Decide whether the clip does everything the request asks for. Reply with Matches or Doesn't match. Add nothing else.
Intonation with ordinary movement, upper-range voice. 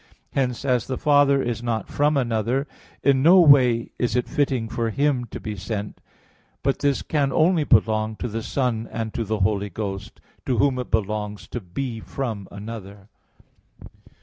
Doesn't match